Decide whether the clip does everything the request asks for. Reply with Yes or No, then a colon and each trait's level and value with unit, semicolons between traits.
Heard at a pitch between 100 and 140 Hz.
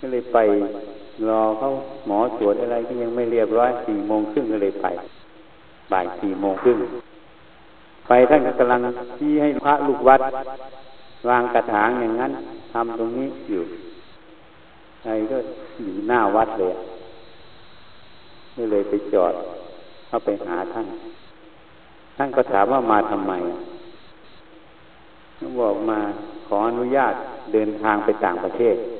Yes: low, 120 Hz